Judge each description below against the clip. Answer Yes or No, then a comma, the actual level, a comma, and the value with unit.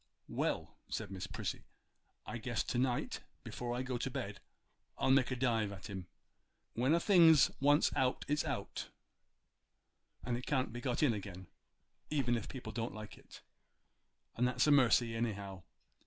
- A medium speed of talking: Yes, average, 160 wpm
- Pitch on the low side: Yes, low, 120 Hz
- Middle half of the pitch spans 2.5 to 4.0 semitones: Yes, average, 3.2 semitones